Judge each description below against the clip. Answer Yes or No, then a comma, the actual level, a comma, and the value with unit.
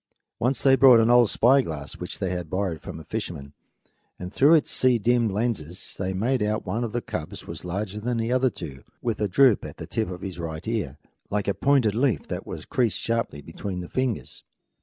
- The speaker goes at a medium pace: No, fast, 225 wpm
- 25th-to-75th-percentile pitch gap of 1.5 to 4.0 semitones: No, average, 5.2 semitones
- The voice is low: Yes, low, 110 Hz